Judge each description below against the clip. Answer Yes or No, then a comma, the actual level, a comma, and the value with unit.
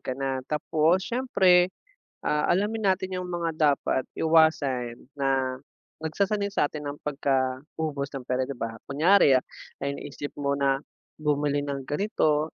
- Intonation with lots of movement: No, average, 3.7 semitones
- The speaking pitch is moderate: Yes, medium, 150 Hz